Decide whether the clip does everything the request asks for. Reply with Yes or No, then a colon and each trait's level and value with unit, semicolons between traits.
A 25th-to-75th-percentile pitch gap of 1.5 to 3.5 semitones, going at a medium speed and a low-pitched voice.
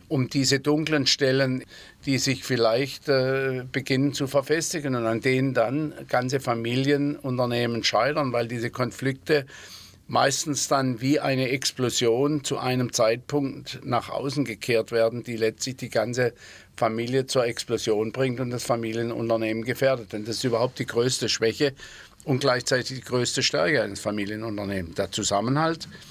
Yes: average, 2.9 semitones; average, 140 wpm; low, 130 Hz